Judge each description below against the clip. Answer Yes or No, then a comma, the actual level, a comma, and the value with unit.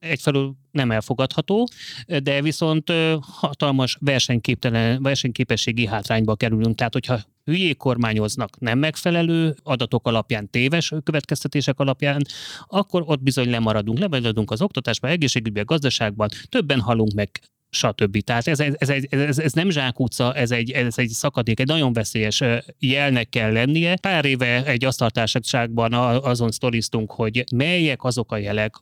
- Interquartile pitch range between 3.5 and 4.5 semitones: Yes, average, 3.8 semitones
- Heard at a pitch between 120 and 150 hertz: Yes, low, 130 Hz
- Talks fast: No, average, 135 wpm